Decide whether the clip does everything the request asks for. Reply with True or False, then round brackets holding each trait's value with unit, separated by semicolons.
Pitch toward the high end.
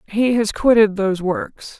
True (210 Hz)